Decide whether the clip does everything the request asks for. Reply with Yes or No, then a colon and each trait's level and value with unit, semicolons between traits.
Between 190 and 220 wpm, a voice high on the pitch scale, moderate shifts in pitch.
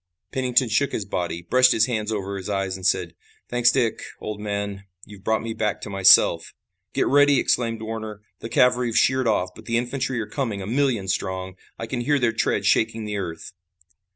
No: average, 200 wpm; low, 110 Hz; average, 3.6 semitones